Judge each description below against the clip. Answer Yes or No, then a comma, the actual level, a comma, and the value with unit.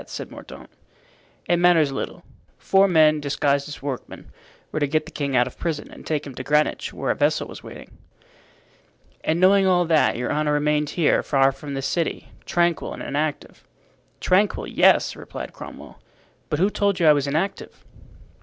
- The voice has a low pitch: No, medium, 150 Hz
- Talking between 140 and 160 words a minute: No, average, 175 wpm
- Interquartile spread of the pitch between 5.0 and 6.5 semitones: No, average, 3.4 semitones